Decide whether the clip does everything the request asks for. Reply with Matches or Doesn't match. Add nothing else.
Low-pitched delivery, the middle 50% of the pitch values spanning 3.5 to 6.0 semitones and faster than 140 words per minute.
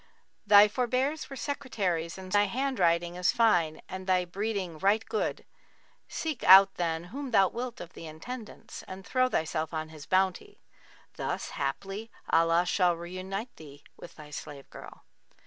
Doesn't match